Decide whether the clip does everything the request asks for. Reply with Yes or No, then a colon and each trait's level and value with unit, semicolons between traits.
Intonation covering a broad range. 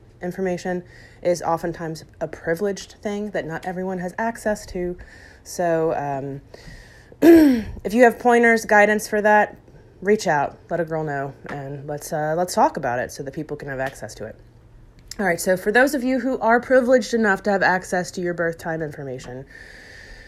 Yes: wide, 6.5 semitones